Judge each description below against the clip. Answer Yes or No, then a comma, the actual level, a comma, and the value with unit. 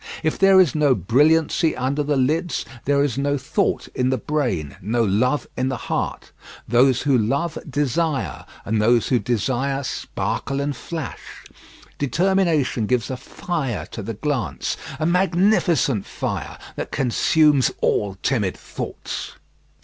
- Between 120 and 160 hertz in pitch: Yes, low, 135 Hz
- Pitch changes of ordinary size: Yes, average, 4.2 semitones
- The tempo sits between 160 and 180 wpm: No, average, 140 wpm